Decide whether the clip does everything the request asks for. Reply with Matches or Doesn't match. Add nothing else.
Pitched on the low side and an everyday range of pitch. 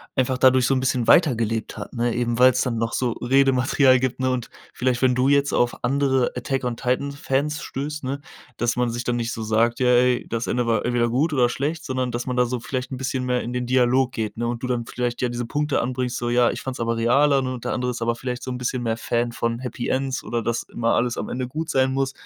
Doesn't match